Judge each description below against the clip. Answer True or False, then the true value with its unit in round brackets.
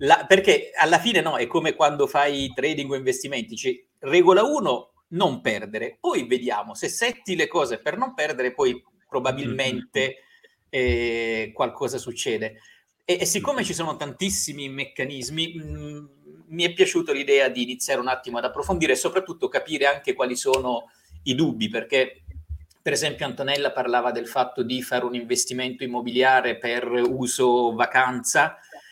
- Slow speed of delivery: False (150 wpm)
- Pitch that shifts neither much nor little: False (7.5 semitones)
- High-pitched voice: False (135 Hz)